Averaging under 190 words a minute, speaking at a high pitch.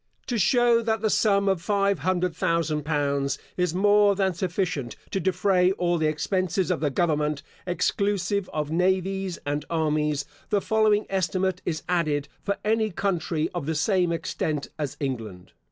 No: average, 155 wpm; medium, 180 Hz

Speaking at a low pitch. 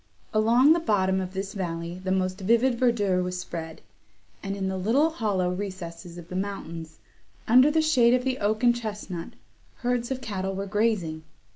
No: high, 200 Hz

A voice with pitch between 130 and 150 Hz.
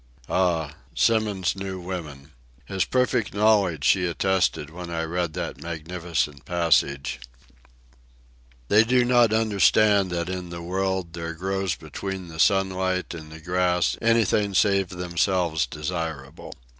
No: very low, 90 Hz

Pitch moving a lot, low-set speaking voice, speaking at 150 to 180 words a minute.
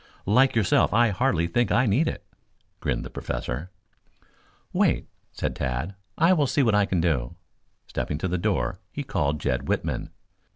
Yes: wide, 8.0 semitones; very low, 95 Hz; average, 165 wpm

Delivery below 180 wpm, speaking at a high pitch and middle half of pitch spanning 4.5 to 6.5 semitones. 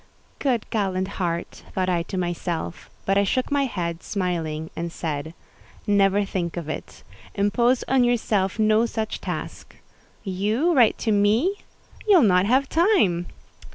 Yes: average, 140 wpm; high, 200 Hz; average, 5.2 semitones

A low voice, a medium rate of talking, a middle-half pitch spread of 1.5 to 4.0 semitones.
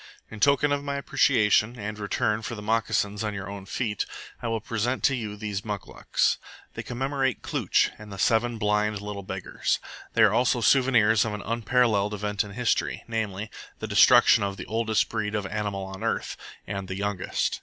Yes: low, 105 Hz; average, 185 wpm; narrow, 2.5 semitones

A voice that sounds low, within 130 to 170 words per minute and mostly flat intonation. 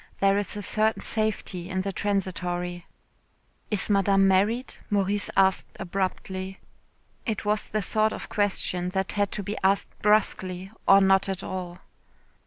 No: high, 195 Hz; average, 145 wpm; narrow, 1.7 semitones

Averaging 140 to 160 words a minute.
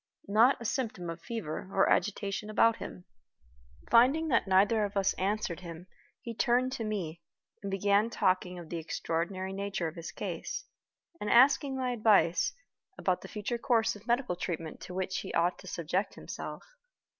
No: average, 170 wpm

